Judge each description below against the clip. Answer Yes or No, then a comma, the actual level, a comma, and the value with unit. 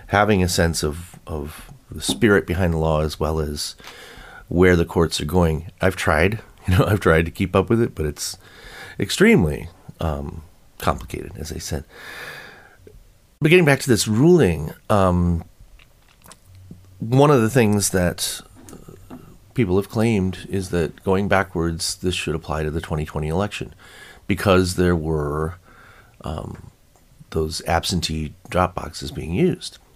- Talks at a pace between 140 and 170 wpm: Yes, average, 145 wpm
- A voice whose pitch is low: Yes, very low, 90 Hz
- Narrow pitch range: No, average, 4.0 semitones